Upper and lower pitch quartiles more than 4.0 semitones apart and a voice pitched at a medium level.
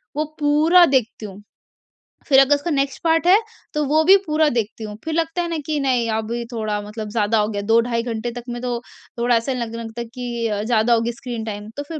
No: average, 4.7 semitones; high, 240 Hz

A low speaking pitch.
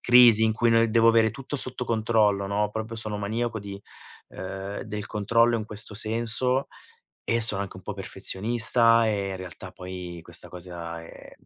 Yes: low, 110 Hz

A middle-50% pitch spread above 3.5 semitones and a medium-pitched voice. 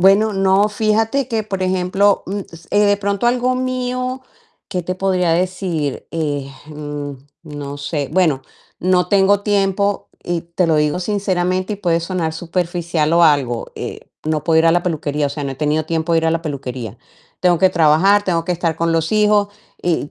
Yes: average, 4.1 semitones; medium, 175 Hz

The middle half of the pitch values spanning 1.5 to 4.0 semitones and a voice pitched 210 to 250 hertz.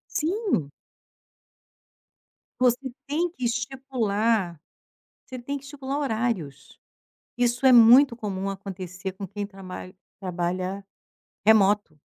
No: wide, 5.4 semitones; high, 220 Hz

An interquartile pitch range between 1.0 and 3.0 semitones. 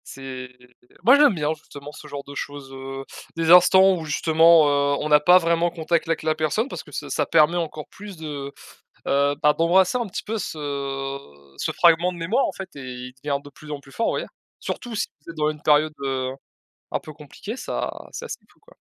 No: average, 3.5 semitones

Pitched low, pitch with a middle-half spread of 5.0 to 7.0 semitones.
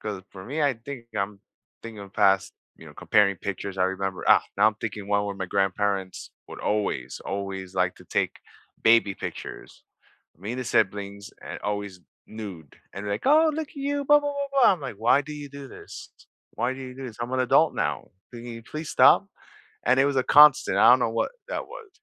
Yes: low, 110 Hz; wide, 5.4 semitones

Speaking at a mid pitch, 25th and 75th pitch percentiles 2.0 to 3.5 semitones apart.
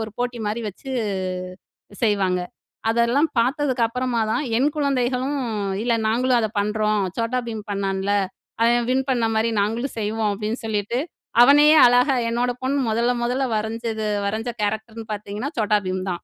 No: high, 230 Hz; average, 2.8 semitones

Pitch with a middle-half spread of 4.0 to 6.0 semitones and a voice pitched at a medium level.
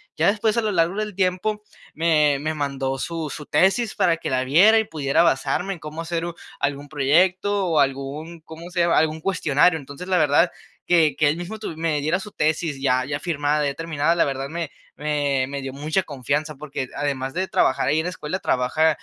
No: average, 3.6 semitones; medium, 155 Hz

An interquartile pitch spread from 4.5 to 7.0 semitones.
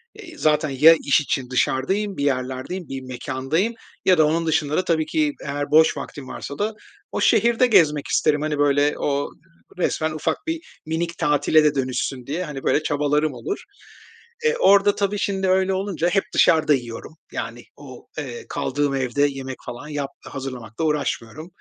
No: average, 4.1 semitones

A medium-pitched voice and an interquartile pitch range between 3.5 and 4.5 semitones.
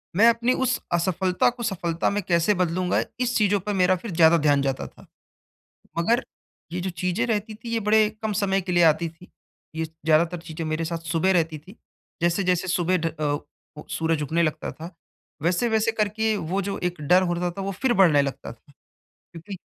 Yes: medium, 180 Hz; average, 3.8 semitones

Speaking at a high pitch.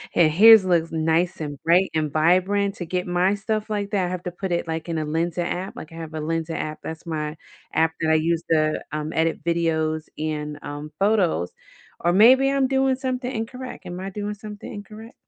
No: medium, 170 Hz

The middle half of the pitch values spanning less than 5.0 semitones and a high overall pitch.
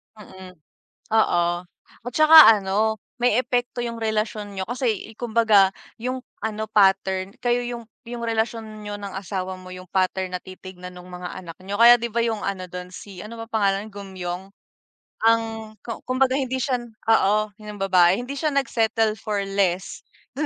Yes: average, 3.4 semitones; high, 215 Hz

